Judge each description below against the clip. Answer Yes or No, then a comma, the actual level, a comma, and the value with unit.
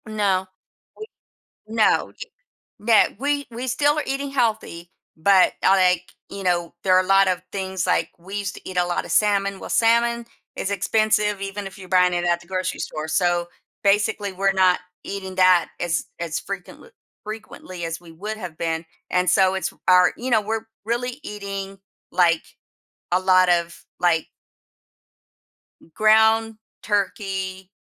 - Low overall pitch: No, high, 195 Hz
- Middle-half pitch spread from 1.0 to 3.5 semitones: Yes, average, 3.1 semitones